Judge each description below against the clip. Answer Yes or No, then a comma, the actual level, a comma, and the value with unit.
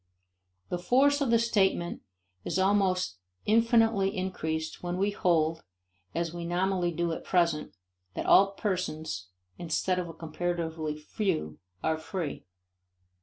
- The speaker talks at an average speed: No, slow, 125 wpm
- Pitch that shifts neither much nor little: Yes, average, 3.4 semitones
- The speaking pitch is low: No, medium, 175 Hz